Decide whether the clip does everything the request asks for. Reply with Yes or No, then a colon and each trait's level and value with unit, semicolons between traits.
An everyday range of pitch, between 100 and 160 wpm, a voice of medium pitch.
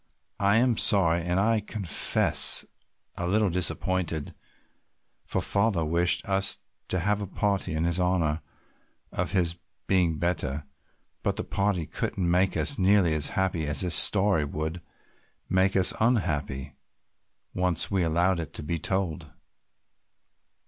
No: average, 3.2 semitones; slow, 135 wpm; very low, 90 Hz